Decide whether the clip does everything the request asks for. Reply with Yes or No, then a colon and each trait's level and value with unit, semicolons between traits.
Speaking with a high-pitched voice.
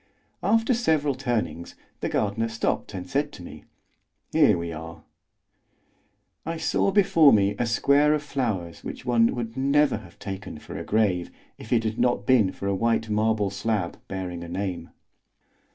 No: low, 110 Hz